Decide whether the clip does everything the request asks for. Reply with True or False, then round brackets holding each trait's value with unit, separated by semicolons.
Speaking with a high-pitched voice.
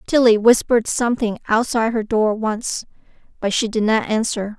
True (225 Hz)